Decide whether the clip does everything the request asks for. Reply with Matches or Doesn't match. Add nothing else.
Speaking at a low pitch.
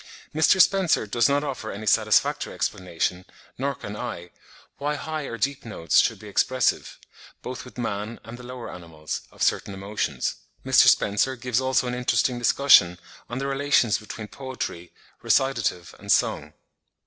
Matches